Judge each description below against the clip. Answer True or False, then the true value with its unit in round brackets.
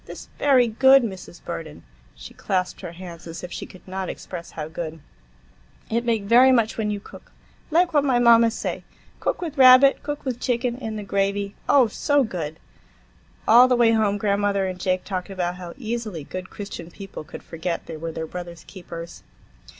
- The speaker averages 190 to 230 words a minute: False (180 wpm)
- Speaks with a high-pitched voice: True (200 Hz)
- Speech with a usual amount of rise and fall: False (5.7 semitones)